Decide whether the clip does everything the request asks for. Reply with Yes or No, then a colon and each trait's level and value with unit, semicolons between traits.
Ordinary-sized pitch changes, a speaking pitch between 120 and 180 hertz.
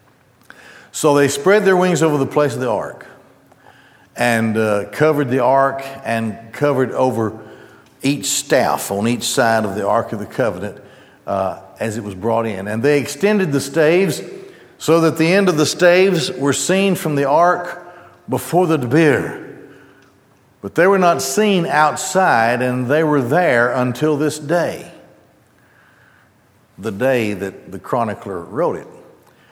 No: wide, 6.4 semitones; medium, 140 Hz